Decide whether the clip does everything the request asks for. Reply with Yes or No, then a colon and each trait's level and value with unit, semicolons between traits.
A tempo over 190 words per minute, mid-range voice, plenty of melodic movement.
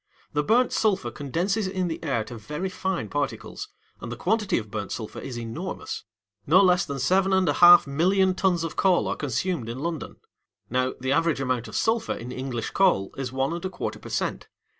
Yes: fast, 205 wpm; medium, 155 Hz; wide, 6.5 semitones